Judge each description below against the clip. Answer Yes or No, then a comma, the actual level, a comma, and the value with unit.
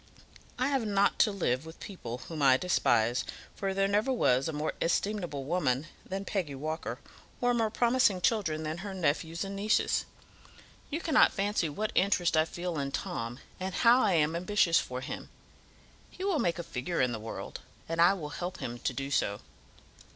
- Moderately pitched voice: Yes, medium, 175 Hz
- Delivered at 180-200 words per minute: Yes, average, 185 wpm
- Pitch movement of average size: No, wide, 5.7 semitones